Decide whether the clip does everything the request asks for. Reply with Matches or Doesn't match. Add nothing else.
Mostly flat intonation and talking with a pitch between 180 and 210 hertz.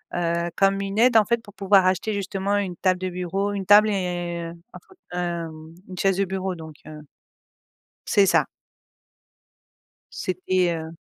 Matches